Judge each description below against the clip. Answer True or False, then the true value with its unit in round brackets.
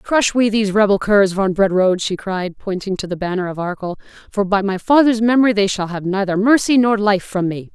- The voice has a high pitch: True (200 Hz)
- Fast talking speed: True (225 wpm)